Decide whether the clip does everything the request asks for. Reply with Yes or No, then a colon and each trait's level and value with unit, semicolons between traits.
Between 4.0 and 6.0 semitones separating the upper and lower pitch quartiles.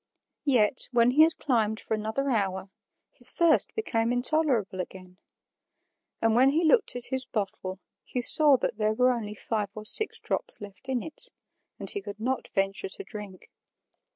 Yes: average, 4.8 semitones